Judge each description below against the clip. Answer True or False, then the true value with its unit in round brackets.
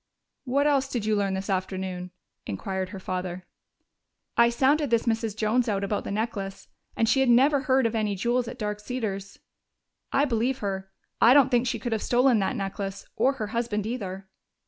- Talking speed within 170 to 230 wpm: True (190 wpm)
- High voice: True (220 Hz)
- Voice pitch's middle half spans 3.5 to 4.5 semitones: True (4.2 semitones)